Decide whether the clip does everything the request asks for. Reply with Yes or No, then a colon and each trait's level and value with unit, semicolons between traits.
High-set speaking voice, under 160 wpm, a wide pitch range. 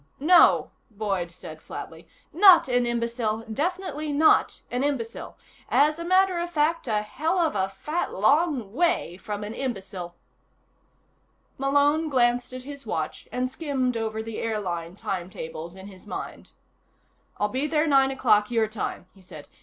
Yes: high, 245 Hz; average, 150 wpm; wide, 6.3 semitones